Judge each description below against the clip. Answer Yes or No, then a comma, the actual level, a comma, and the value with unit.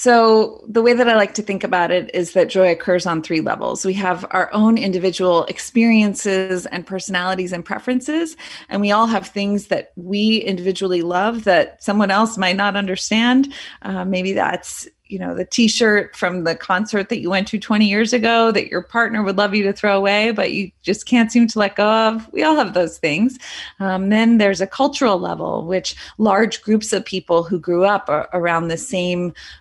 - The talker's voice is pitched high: Yes, high, 200 Hz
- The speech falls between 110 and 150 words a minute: No, fast, 205 wpm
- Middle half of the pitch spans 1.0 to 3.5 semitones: Yes, average, 3.2 semitones